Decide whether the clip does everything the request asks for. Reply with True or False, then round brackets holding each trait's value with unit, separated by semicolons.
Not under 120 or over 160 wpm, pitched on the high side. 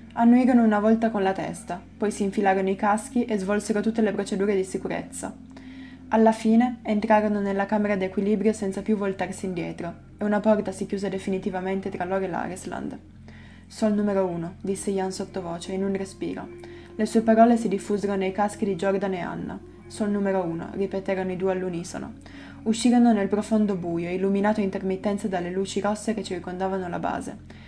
False (170 wpm; 200 Hz)